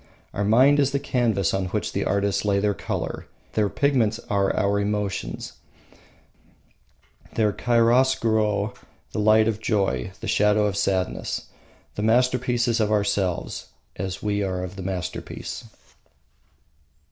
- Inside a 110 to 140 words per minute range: Yes, slow, 135 wpm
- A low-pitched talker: Yes, low, 105 Hz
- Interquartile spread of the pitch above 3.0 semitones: No, narrow, 2.5 semitones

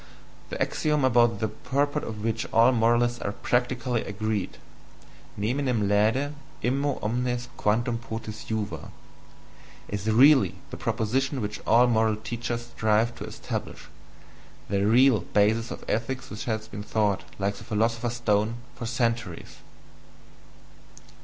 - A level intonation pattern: Yes, narrow, 2.3 semitones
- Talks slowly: Yes, slow, 130 wpm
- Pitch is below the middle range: Yes, low, 115 Hz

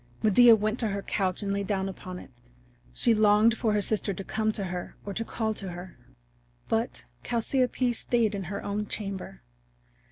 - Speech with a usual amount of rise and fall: No, narrow, 2.3 semitones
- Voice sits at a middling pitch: No, high, 210 Hz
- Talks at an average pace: Yes, average, 185 wpm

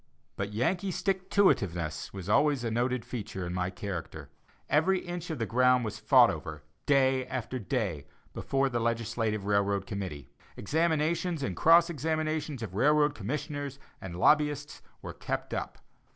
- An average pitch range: No, wide, 7.0 semitones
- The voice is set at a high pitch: No, low, 125 Hz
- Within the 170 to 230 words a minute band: No, average, 155 wpm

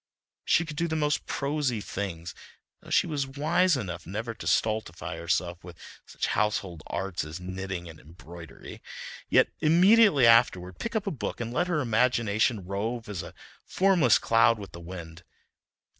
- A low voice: Yes, low, 110 Hz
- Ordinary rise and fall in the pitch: No, wide, 8.5 semitones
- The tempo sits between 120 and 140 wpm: No, average, 160 wpm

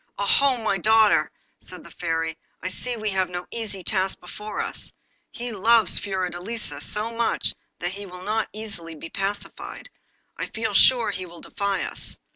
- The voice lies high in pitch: Yes, high, 200 Hz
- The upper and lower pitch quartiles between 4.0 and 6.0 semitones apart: No, average, 3.4 semitones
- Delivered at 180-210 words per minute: No, average, 165 wpm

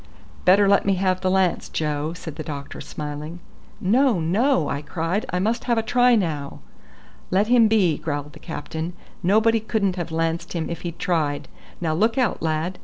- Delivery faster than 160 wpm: Yes, average, 180 wpm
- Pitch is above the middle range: No, medium, 180 Hz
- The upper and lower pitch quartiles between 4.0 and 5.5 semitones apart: Yes, average, 4.9 semitones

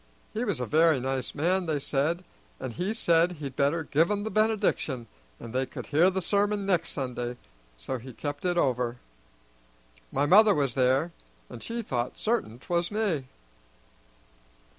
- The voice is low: No, medium, 155 Hz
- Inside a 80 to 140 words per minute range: No, average, 160 wpm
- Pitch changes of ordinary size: No, wide, 6.3 semitones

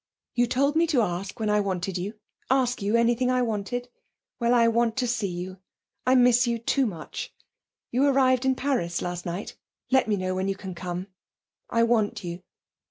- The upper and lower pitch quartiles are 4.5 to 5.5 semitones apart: Yes, average, 4.9 semitones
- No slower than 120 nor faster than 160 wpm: No, average, 195 wpm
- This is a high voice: Yes, high, 230 Hz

